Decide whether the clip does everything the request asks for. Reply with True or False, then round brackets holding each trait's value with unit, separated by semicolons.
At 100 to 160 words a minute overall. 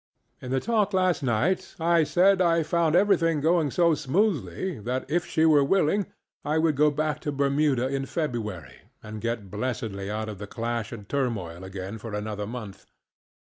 False (170 wpm)